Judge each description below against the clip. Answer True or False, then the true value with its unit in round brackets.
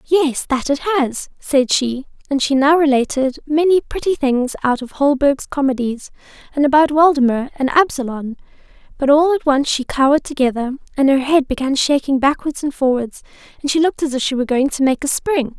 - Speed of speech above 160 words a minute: True (185 wpm)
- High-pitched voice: True (280 Hz)